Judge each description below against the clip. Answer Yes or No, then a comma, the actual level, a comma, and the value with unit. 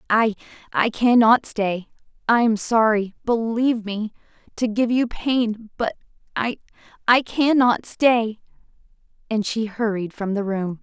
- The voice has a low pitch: No, high, 225 Hz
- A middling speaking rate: No, slow, 120 wpm